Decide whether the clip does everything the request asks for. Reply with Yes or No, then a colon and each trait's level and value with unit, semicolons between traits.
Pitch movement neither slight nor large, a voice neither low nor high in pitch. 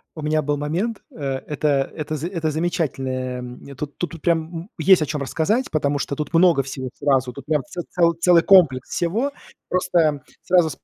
Yes: average, 3.7 semitones; medium, 155 Hz